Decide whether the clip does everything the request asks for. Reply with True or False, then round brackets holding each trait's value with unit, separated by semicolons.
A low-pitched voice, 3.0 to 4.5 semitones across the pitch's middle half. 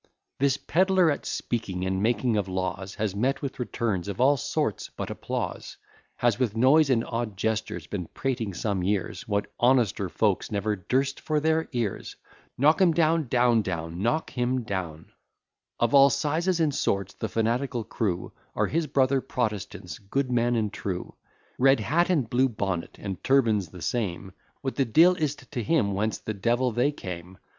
False (120 Hz; 5.5 semitones)